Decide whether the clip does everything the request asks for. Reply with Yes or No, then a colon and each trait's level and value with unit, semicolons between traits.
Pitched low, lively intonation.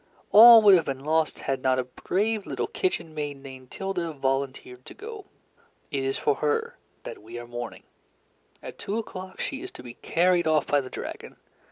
No: medium, 150 Hz; wide, 6.5 semitones